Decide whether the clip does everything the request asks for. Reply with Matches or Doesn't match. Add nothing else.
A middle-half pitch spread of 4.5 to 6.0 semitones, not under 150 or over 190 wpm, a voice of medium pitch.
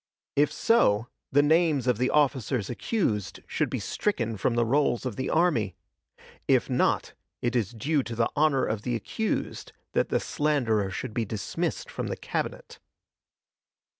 Doesn't match